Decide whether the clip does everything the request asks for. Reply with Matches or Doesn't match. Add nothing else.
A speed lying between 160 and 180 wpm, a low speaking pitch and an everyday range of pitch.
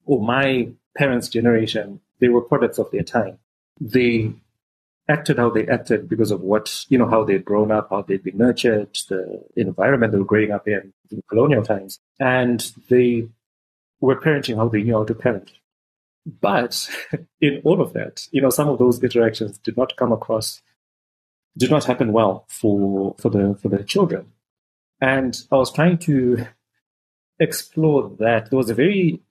Matches